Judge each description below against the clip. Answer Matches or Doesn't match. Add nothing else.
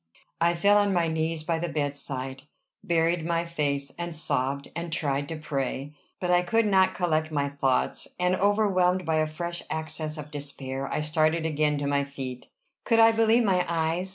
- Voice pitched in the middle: Matches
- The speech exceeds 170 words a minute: Matches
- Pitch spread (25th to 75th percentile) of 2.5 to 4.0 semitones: Matches